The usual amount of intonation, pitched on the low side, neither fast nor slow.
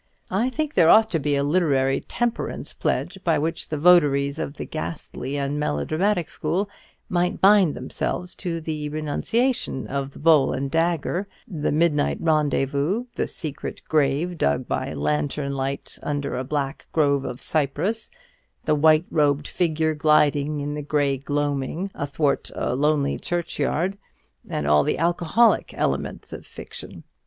No: average, 3.5 semitones; medium, 150 Hz; average, 145 wpm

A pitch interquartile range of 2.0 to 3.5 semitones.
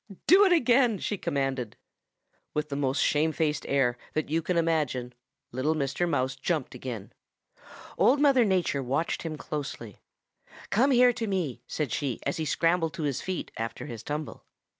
No: wide, 5.5 semitones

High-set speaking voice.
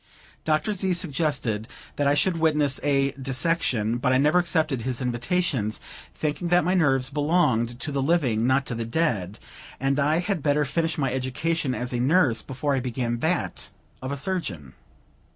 No: medium, 140 Hz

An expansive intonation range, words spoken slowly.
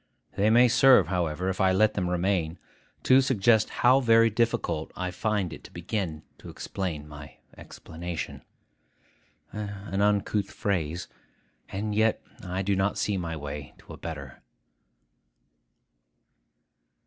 No: average, 3.8 semitones; slow, 130 wpm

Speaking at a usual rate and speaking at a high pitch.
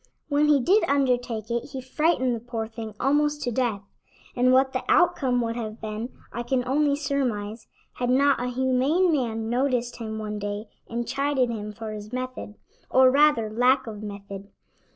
Yes: average, 175 wpm; high, 245 Hz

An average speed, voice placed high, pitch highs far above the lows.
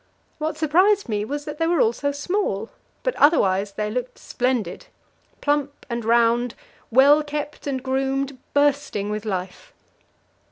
No: average, 145 wpm; very high, 270 Hz; average, 4.6 semitones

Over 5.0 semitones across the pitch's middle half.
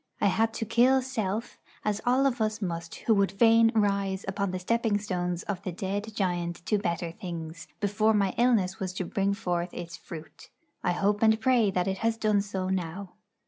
No: average, 3.3 semitones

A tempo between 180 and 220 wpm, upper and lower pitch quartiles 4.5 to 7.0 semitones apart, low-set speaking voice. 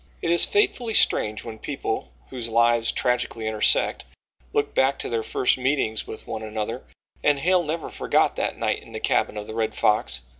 Yes: average, 185 wpm; average, 4.8 semitones; low, 120 Hz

